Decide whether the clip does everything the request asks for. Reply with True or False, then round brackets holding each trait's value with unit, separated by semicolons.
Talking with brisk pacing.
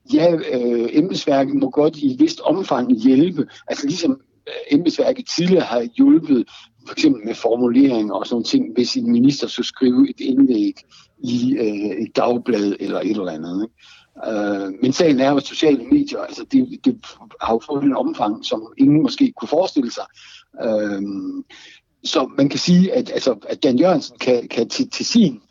False (175 wpm)